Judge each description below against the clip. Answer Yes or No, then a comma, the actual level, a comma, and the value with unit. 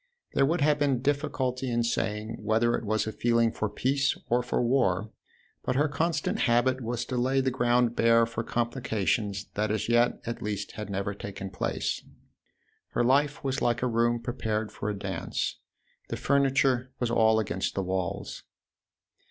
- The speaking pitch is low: Yes, low, 120 Hz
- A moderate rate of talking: Yes, average, 170 wpm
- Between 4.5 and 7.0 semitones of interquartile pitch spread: No, average, 3.2 semitones